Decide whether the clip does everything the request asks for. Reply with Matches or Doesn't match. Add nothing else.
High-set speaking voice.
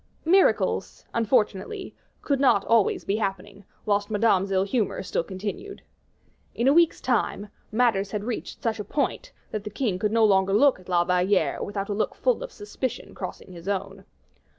Matches